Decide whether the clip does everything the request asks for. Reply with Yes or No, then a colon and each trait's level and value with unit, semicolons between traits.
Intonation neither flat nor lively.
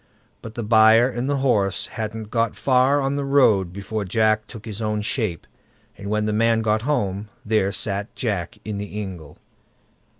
No: narrow, 2.3 semitones